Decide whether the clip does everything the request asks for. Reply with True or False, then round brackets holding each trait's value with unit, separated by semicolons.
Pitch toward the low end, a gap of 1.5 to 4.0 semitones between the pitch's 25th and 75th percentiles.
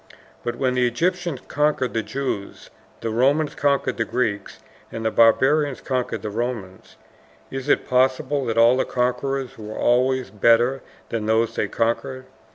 True (125 Hz; 2.9 semitones)